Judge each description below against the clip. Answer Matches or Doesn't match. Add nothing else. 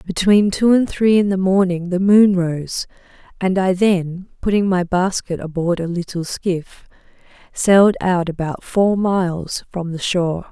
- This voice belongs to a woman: Matches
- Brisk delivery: Doesn't match